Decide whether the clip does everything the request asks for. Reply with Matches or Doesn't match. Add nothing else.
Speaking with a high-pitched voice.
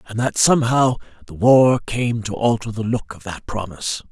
Doesn't match